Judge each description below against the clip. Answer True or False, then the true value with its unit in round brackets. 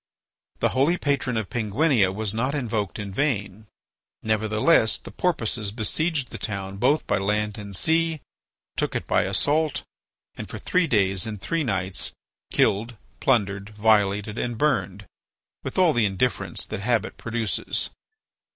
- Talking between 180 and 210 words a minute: False (140 wpm)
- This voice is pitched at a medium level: False (110 Hz)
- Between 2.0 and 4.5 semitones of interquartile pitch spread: False (4.9 semitones)